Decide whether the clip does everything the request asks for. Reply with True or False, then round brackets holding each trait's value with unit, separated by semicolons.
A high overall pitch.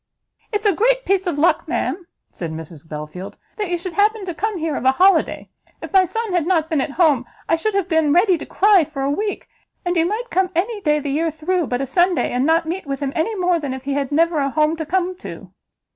True (335 Hz)